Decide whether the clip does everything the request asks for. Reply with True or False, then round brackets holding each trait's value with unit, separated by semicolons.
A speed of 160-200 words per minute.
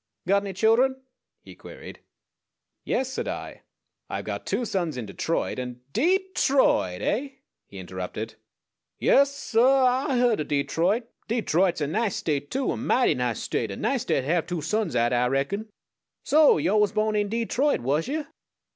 True (180 wpm)